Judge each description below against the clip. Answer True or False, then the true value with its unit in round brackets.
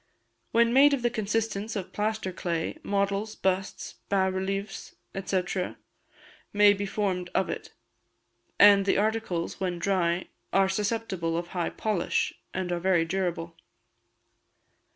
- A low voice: False (195 Hz)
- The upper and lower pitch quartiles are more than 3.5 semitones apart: False (2.7 semitones)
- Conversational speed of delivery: False (130 wpm)